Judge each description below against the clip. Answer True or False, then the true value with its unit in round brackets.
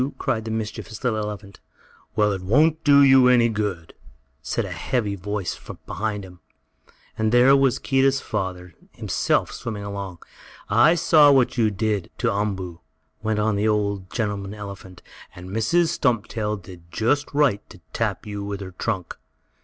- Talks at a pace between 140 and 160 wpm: True (155 wpm)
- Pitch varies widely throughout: False (3.6 semitones)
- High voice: False (105 Hz)